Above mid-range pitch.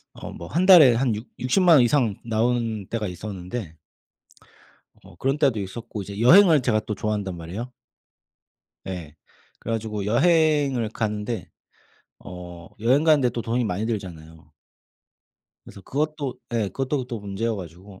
No: low, 115 Hz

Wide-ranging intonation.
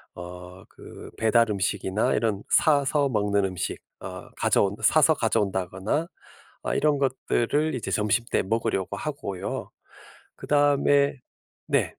Yes: wide, 6.6 semitones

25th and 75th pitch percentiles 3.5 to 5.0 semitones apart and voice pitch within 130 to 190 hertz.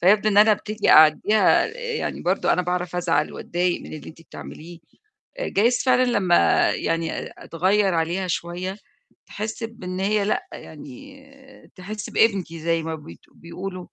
Yes: average, 4.2 semitones; medium, 185 Hz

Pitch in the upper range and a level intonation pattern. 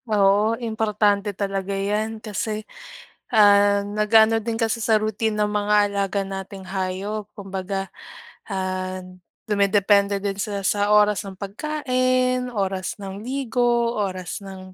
Yes: high, 205 Hz; narrow, 2.0 semitones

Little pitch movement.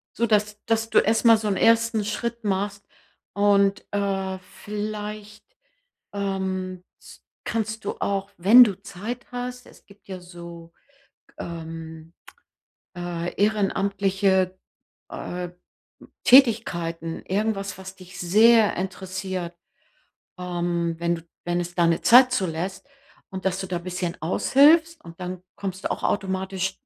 No: average, 3.0 semitones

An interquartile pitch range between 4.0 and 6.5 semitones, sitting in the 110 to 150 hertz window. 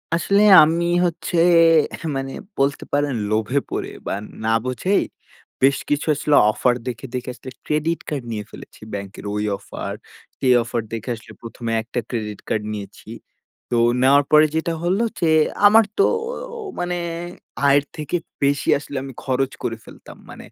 Yes: average, 4.5 semitones; low, 135 Hz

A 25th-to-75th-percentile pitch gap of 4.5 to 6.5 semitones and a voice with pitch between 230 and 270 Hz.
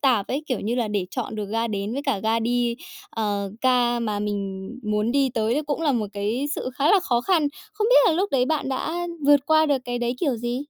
Yes: average, 4.9 semitones; high, 245 Hz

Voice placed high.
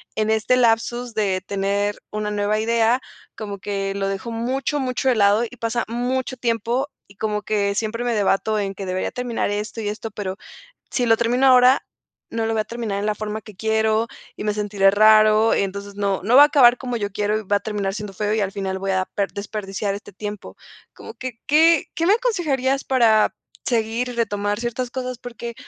Yes: high, 220 Hz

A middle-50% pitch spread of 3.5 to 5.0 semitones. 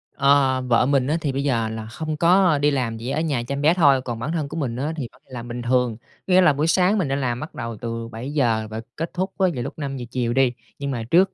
Yes: average, 4.4 semitones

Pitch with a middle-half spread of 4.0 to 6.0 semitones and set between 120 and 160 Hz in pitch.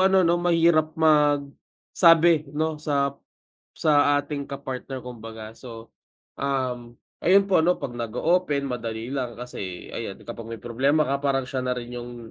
Yes: average, 4.5 semitones; medium, 140 Hz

